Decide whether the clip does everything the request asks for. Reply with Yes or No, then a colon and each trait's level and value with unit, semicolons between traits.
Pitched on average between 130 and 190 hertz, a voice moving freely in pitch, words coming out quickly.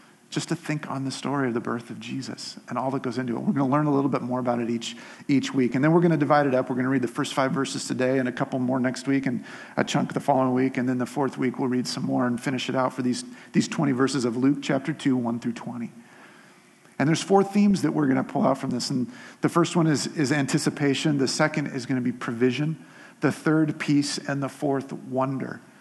No: low, 135 Hz; narrow, 2.6 semitones; fast, 270 wpm